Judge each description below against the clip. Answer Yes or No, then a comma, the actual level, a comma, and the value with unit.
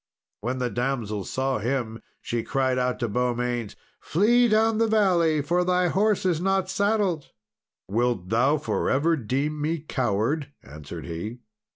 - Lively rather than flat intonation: Yes, wide, 6.9 semitones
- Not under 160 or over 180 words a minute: No, average, 150 wpm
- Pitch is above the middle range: No, low, 135 Hz